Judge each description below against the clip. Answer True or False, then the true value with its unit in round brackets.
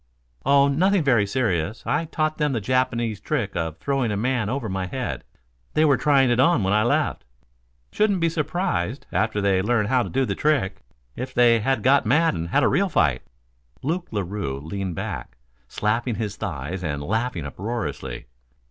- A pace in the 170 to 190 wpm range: True (175 wpm)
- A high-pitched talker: False (115 Hz)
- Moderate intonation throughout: False (6.3 semitones)